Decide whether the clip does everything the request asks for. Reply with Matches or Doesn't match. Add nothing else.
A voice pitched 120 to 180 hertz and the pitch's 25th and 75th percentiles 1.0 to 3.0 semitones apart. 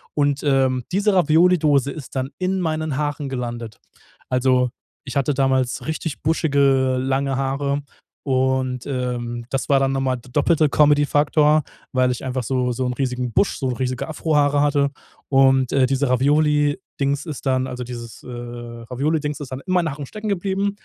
Matches